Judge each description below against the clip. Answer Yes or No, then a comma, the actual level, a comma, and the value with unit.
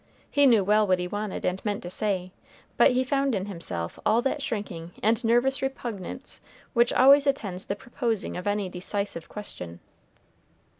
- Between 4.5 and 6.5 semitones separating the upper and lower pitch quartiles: Yes, average, 4.8 semitones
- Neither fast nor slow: Yes, average, 165 wpm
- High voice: Yes, high, 210 Hz